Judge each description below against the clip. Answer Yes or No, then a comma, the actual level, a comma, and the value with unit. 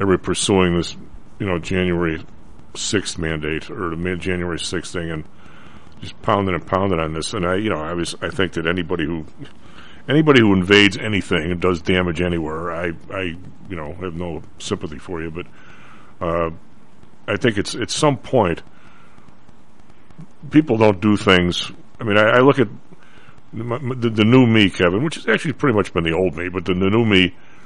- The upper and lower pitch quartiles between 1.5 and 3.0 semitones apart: No, average, 3.6 semitones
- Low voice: Yes, very low, 90 Hz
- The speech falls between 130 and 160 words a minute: No, average, 190 wpm